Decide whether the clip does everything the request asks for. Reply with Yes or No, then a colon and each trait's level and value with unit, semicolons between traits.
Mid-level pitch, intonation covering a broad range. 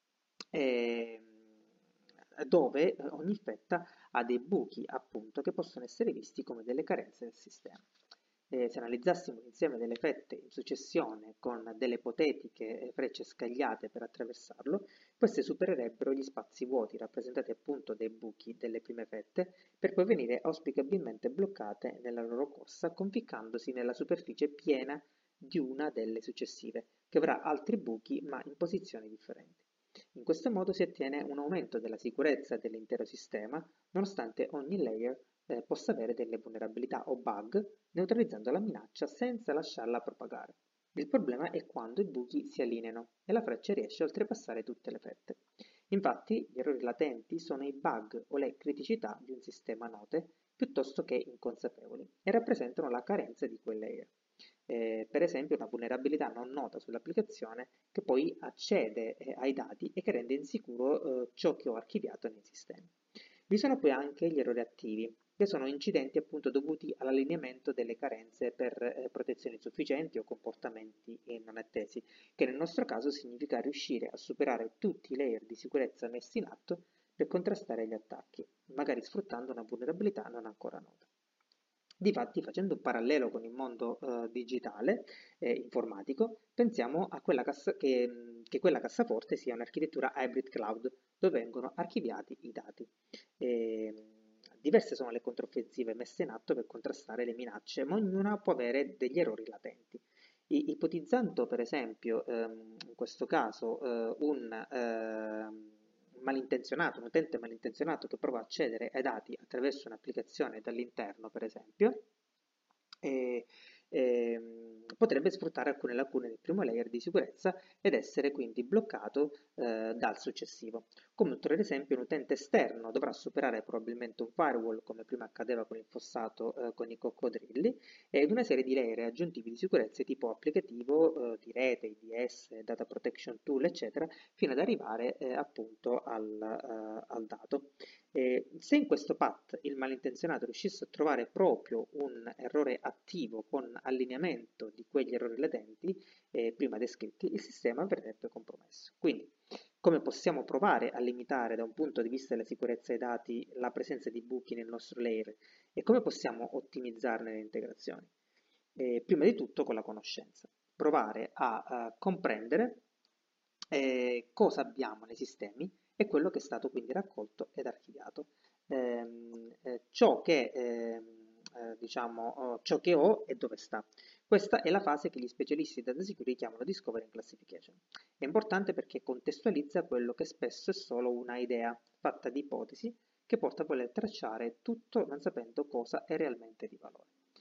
No: low, 125 Hz; wide, 5.7 semitones